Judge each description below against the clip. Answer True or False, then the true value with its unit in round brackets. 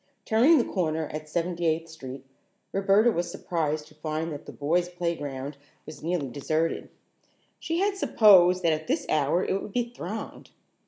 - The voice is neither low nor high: True (165 Hz)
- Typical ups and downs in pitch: True (3.8 semitones)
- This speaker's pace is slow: False (165 wpm)